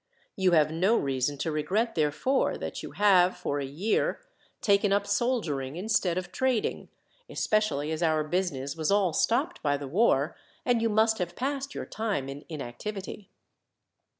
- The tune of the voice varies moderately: No, wide, 6.4 semitones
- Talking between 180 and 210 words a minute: No, average, 160 wpm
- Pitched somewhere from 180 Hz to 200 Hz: Yes, medium, 185 Hz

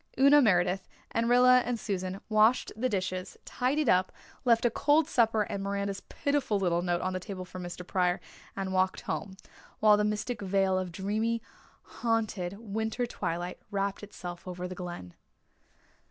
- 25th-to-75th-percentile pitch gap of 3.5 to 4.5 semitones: Yes, average, 3.8 semitones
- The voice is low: No, high, 200 Hz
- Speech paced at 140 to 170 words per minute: Yes, average, 160 wpm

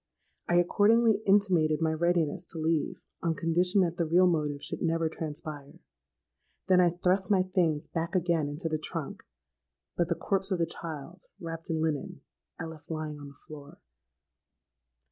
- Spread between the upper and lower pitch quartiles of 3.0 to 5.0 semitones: No, narrow, 2.5 semitones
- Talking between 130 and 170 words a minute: Yes, average, 165 wpm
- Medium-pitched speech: Yes, medium, 165 Hz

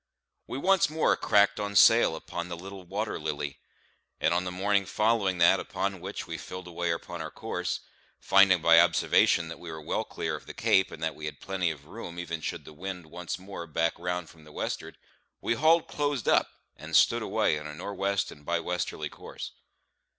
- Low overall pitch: Yes, very low, 90 Hz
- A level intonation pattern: No, average, 3.2 semitones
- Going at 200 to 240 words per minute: Yes, fast, 205 wpm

